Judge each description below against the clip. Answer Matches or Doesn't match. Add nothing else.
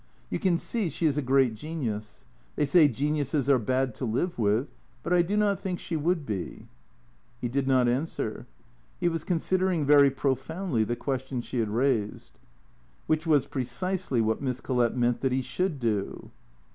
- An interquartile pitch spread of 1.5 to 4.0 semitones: Doesn't match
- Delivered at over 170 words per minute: Matches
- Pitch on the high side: Doesn't match